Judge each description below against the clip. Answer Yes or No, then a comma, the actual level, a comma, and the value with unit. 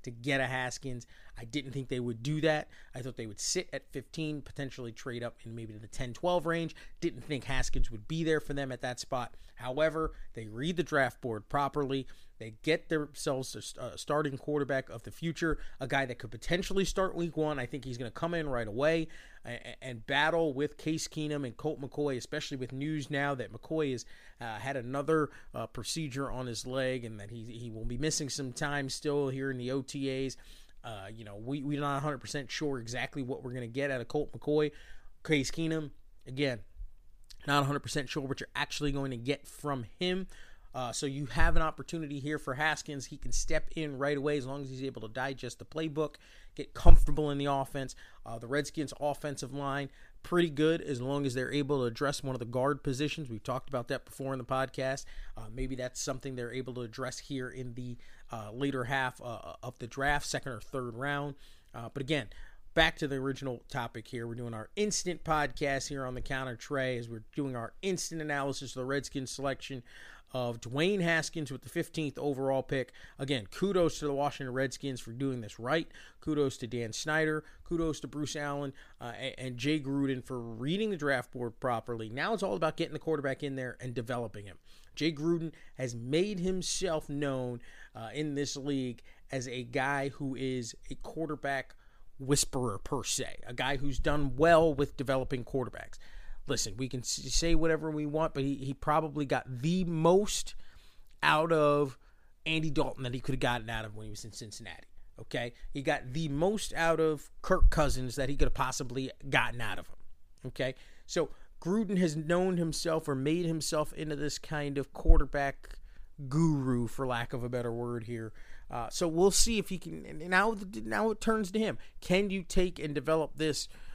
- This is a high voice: No, medium, 140 Hz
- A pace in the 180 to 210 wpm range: Yes, average, 200 wpm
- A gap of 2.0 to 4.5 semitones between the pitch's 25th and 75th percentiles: Yes, average, 3.5 semitones